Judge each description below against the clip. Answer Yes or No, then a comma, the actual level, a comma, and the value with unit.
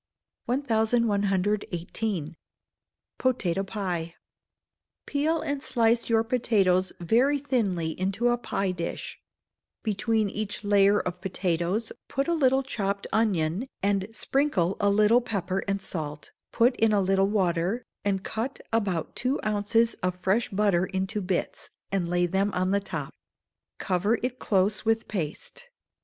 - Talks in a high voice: Yes, high, 205 Hz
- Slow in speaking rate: Yes, slow, 130 wpm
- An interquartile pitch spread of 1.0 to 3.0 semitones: No, average, 3.7 semitones